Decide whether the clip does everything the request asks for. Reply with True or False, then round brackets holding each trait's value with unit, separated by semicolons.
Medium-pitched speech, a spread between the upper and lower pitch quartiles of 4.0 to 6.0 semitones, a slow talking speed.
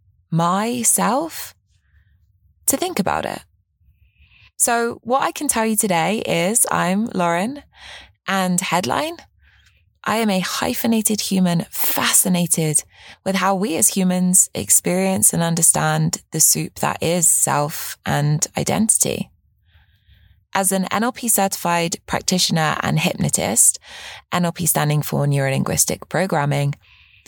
False (175 Hz; 8.9 semitones; 110 wpm)